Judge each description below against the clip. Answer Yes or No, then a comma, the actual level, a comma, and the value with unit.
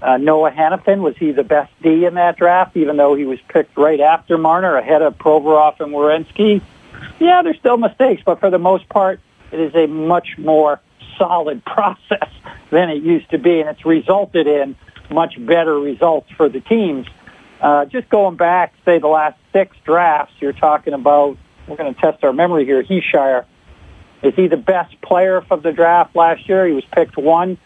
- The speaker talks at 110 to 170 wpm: No, average, 195 wpm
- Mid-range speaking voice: Yes, medium, 160 Hz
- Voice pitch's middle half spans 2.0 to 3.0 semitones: No, average, 3.5 semitones